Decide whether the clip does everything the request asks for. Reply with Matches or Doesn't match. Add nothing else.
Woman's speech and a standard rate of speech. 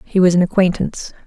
Matches